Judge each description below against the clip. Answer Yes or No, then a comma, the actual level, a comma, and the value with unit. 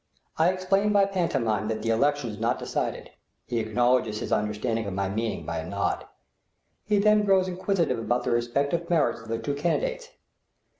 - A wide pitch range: Yes, wide, 8.7 semitones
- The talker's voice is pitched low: Yes, low, 125 Hz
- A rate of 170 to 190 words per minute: Yes, average, 180 wpm